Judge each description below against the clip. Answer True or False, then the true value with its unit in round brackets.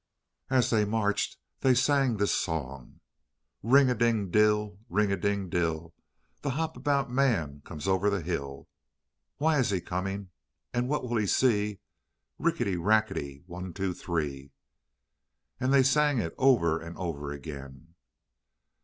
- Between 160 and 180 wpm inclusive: False (145 wpm)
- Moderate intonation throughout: False (6.9 semitones)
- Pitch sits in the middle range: False (100 Hz)